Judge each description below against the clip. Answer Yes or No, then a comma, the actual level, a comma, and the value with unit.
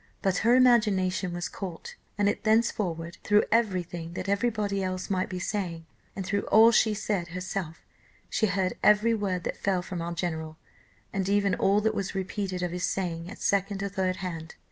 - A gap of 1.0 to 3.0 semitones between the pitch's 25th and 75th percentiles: Yes, narrow, 2.6 semitones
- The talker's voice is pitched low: No, high, 190 Hz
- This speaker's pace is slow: No, average, 190 wpm